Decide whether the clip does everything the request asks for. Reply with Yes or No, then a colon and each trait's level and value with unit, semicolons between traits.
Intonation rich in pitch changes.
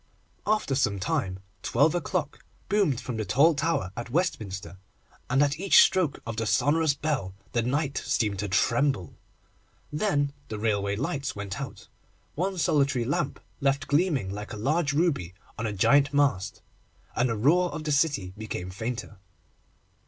Yes: wide, 6.1 semitones